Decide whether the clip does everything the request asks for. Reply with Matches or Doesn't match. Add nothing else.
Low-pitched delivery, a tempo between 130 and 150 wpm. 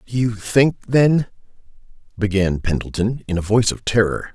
Matches